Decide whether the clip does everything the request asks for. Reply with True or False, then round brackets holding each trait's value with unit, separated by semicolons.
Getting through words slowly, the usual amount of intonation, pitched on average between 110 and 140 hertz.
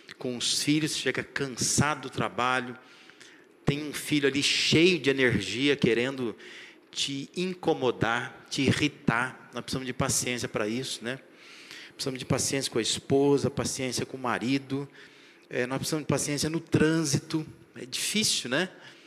False (145 wpm; 3.2 semitones; 135 Hz)